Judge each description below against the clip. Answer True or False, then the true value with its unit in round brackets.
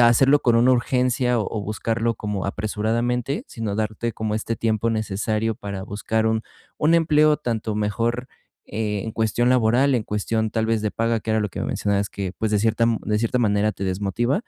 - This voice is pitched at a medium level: False (110 Hz)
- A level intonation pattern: True (2.1 semitones)